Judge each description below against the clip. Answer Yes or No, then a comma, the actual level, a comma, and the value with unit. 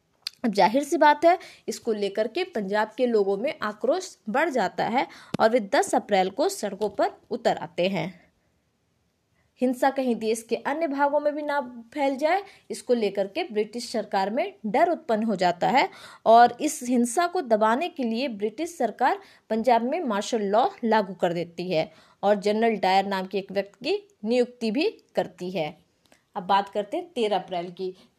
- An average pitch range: No, wide, 6.0 semitones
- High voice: Yes, high, 225 Hz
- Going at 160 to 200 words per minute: Yes, average, 175 wpm